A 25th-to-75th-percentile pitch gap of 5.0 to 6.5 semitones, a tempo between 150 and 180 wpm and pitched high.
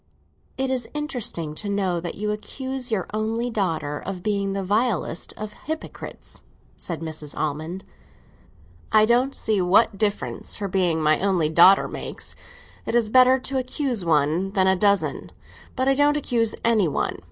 Yes: wide, 5.4 semitones; average, 160 wpm; high, 200 Hz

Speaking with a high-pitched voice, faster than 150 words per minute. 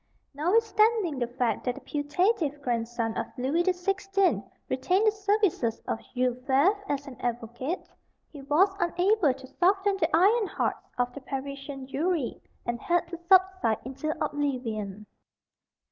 No: very high, 290 Hz; average, 145 wpm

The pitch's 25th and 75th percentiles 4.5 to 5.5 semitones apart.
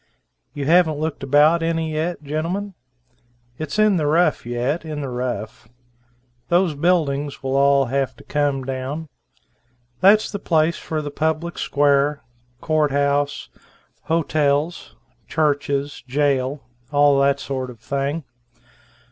No: narrow, 2.5 semitones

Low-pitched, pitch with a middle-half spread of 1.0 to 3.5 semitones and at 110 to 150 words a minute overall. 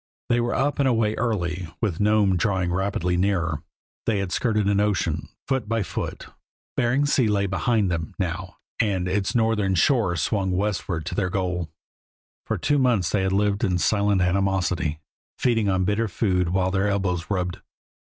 No: low, 100 Hz; average, 3.0 semitones; average, 170 wpm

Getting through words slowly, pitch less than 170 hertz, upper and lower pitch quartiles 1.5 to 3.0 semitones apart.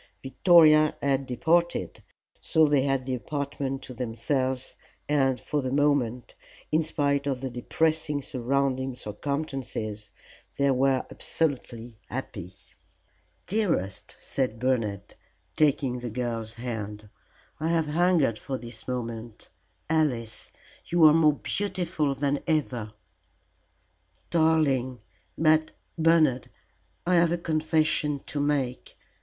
No: slow, 110 wpm; low, 135 Hz; average, 3.9 semitones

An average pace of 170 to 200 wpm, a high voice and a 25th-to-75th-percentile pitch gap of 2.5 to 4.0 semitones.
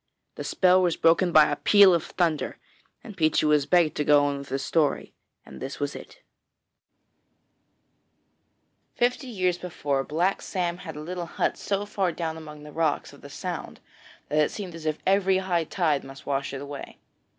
No: average, 185 wpm; medium, 165 Hz; average, 3.7 semitones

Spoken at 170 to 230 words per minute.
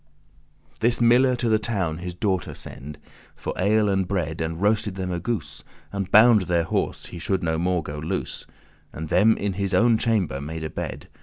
Yes: average, 190 wpm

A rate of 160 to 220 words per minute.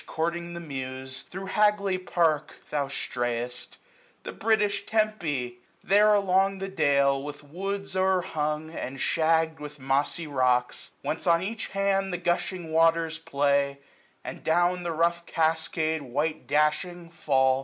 No: average, 140 wpm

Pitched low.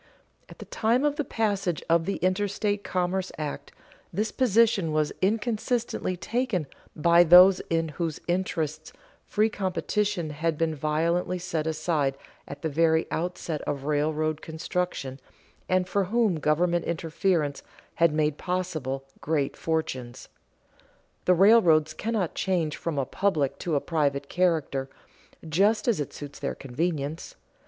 No: medium, 170 Hz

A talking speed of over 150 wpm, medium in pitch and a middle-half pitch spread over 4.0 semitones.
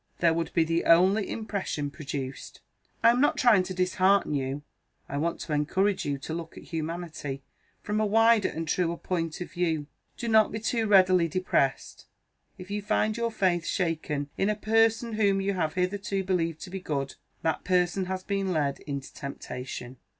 Yes: average, 180 wpm; medium, 180 Hz; average, 4.4 semitones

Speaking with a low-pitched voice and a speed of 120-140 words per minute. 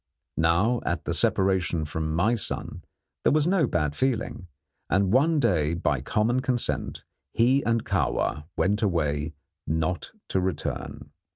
Yes: very low, 95 Hz; slow, 135 wpm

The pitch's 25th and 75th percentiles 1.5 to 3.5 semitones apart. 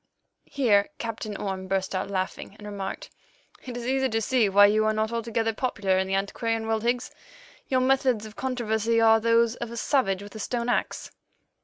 Yes: average, 2.7 semitones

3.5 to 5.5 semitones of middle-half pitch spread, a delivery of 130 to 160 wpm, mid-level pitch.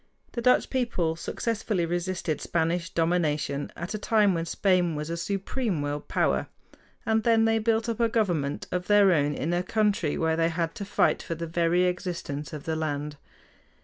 No: average, 4.4 semitones; average, 180 wpm; medium, 175 Hz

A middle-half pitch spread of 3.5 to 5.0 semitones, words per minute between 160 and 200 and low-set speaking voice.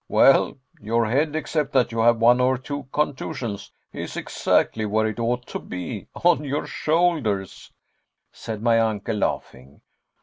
No: average, 4.0 semitones; average, 145 wpm; low, 115 Hz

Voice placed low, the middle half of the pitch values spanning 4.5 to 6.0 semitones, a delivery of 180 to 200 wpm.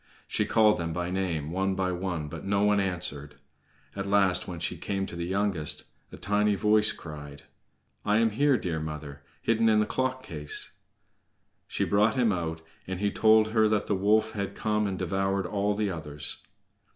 No: low, 100 Hz; average, 3.8 semitones; average, 185 wpm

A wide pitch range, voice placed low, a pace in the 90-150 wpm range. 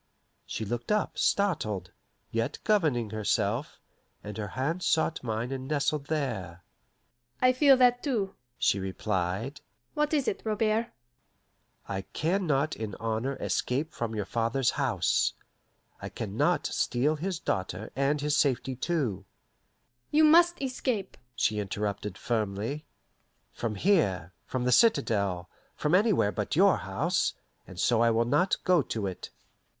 Yes: wide, 8.9 semitones; low, 130 Hz; average, 140 wpm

